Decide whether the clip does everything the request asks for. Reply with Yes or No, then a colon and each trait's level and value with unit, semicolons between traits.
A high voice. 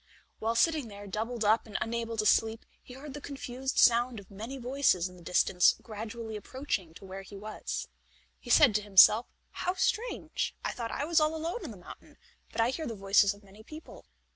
Yes: high, 230 Hz